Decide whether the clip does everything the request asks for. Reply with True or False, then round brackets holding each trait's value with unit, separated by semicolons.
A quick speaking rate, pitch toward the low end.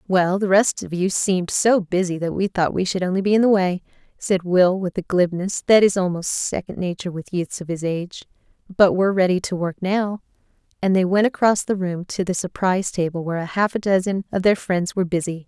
False (225 wpm; 185 Hz)